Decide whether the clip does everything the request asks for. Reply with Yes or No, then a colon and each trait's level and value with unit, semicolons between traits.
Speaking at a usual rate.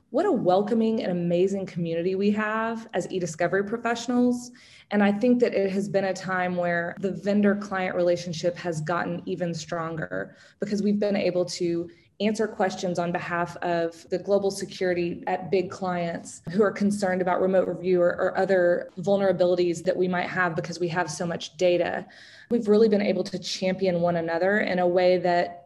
Yes: average, 180 wpm